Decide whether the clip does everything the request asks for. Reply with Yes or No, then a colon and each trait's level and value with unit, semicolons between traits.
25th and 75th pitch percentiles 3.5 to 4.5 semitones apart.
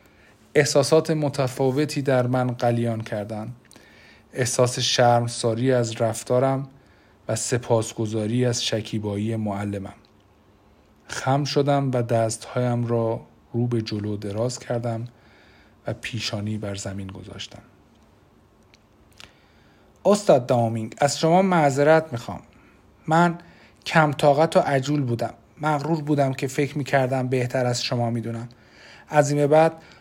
Yes: average, 4.1 semitones